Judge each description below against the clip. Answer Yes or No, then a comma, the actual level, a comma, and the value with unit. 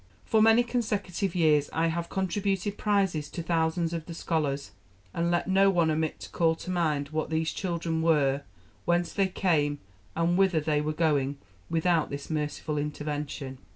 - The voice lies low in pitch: No, medium, 165 Hz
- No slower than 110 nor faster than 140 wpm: No, average, 165 wpm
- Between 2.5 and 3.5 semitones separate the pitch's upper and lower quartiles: Yes, average, 3.2 semitones